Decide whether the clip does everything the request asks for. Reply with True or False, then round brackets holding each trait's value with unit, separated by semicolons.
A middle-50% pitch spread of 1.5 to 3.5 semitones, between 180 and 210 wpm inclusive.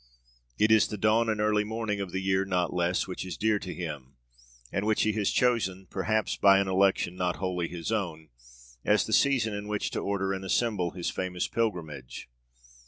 True (3.0 semitones; 195 wpm)